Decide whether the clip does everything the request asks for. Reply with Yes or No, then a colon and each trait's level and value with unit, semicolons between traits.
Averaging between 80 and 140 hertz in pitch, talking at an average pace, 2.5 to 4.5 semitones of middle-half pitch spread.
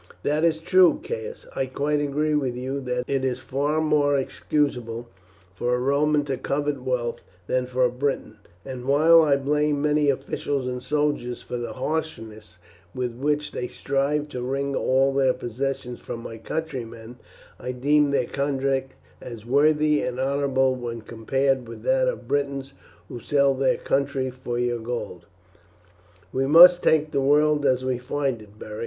Yes: low, 135 Hz; average, 165 wpm; average, 2.9 semitones